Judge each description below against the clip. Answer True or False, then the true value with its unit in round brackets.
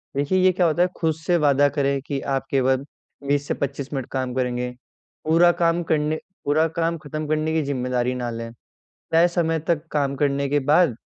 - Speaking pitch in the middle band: True (145 Hz)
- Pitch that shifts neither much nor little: True (3.2 semitones)